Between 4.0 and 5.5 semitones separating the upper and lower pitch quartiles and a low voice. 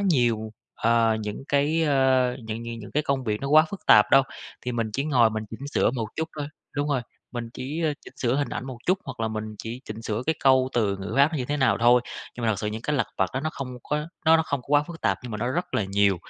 Yes: average, 4.5 semitones; low, 125 Hz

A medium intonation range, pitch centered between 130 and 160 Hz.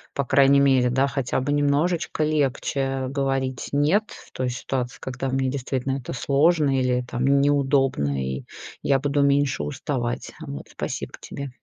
No: narrow, 1.9 semitones; low, 135 Hz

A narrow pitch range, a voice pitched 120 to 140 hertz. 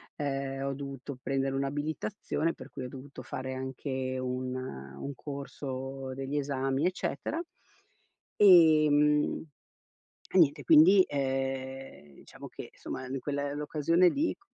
Yes: narrow, 2.0 semitones; low, 135 Hz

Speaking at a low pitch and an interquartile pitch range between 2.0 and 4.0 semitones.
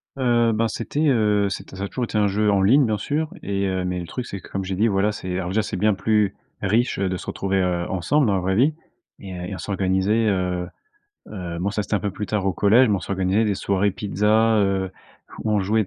Yes: low, 100 Hz; narrow, 2.4 semitones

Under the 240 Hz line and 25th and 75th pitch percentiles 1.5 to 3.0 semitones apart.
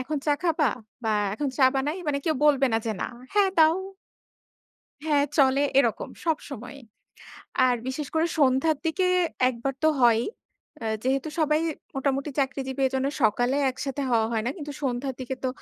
No: very high, 275 Hz; average, 2.7 semitones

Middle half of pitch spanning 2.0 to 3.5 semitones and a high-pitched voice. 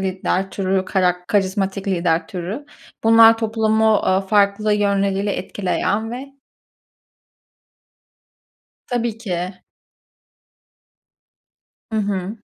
Yes: average, 2.7 semitones; high, 200 Hz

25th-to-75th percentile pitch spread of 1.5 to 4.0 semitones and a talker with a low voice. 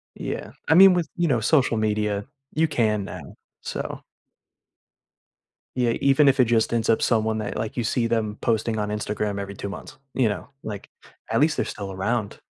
Yes: average, 3.5 semitones; low, 110 Hz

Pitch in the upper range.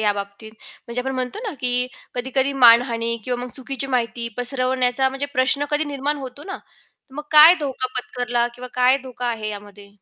Yes: very high, 250 Hz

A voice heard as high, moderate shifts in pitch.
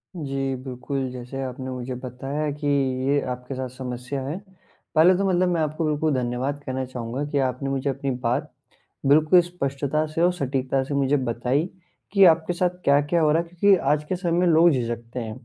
No: medium, 140 Hz; average, 3.6 semitones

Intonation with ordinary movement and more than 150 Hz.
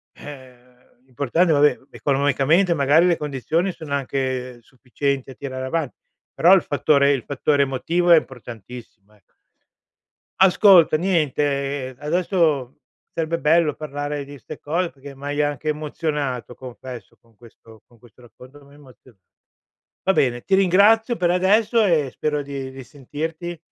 No: average, 4.1 semitones; medium, 145 Hz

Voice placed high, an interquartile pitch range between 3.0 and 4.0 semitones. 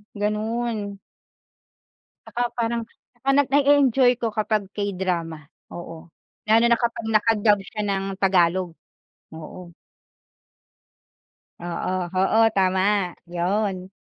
Yes: high, 205 Hz; average, 3.6 semitones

